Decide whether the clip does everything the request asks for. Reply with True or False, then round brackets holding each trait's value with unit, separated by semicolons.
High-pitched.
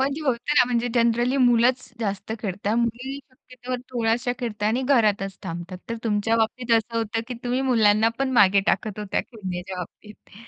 True (230 Hz)